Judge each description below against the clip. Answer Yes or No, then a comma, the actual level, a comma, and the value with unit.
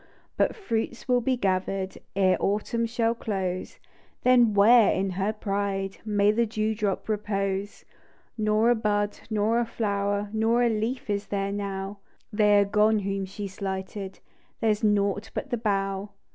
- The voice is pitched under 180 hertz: No, high, 205 Hz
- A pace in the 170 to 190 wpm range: No, average, 160 wpm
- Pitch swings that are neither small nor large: No, narrow, 2.0 semitones